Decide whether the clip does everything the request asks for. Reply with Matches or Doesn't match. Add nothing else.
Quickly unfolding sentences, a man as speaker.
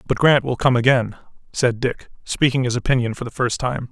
Matches